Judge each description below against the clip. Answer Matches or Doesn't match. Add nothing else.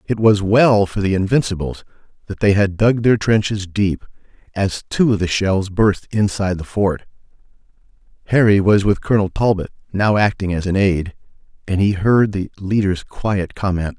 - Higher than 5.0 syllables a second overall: Doesn't match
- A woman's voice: Doesn't match